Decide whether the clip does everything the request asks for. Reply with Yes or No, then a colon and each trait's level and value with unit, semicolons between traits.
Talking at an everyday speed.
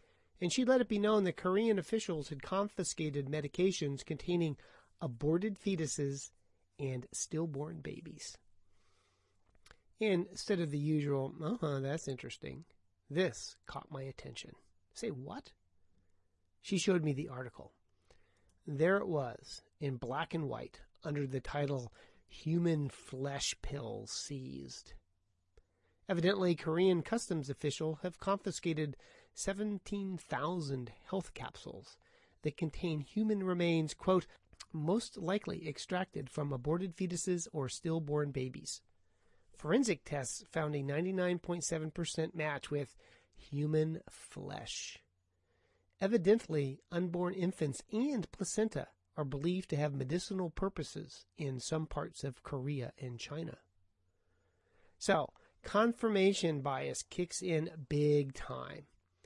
No: slow, 110 wpm